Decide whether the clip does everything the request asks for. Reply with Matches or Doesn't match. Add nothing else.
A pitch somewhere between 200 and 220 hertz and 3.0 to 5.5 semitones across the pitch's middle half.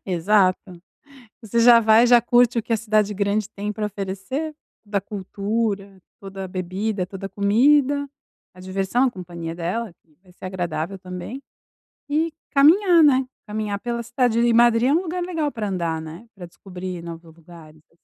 Matches